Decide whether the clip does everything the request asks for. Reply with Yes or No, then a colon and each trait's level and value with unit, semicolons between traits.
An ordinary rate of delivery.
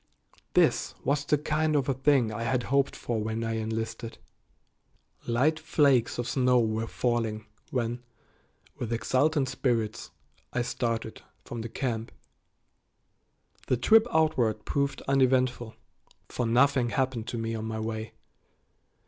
No: slow, 130 wpm